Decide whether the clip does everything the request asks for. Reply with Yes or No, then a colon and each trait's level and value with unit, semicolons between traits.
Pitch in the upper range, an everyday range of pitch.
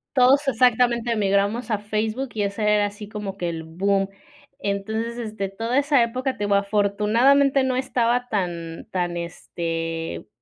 Yes: high, 210 Hz; average, 3.6 semitones